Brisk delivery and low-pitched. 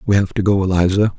Yes: fast, 255 wpm; very low, 95 Hz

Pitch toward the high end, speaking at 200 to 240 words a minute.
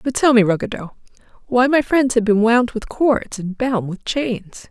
Yes: high, 230 Hz; fast, 205 wpm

